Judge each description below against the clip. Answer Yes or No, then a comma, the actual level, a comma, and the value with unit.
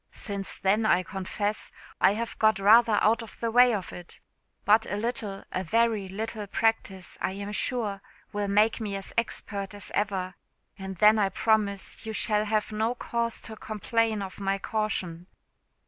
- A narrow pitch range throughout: Yes, narrow, 2.2 semitones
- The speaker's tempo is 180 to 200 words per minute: No, average, 170 wpm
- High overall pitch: Yes, high, 210 Hz